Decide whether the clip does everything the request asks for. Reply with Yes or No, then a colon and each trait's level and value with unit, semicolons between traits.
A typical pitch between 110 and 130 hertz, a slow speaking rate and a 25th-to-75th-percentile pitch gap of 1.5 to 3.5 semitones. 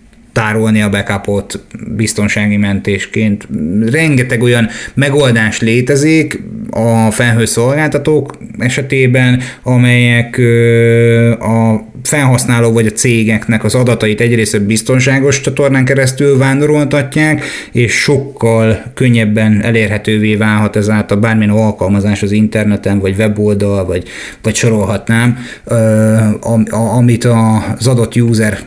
Yes: low, 115 Hz; slow, 95 wpm; average, 2.7 semitones